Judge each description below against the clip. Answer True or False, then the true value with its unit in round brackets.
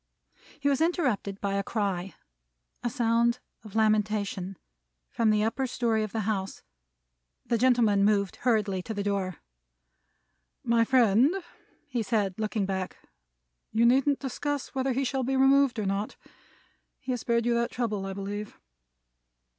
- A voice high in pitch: True (225 Hz)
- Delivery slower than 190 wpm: True (145 wpm)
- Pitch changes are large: False (4.0 semitones)